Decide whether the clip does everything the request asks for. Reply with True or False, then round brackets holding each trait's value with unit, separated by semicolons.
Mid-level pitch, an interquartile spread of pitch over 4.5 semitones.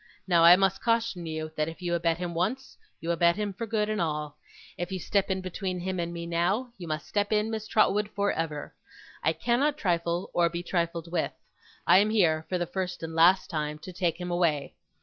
False (175 Hz; 3.3 semitones)